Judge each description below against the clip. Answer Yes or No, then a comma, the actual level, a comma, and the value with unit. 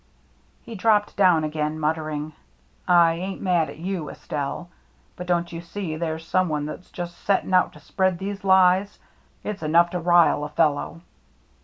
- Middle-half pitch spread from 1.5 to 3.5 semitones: Yes, average, 3.1 semitones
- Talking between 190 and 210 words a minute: No, average, 170 wpm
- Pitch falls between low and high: Yes, medium, 170 Hz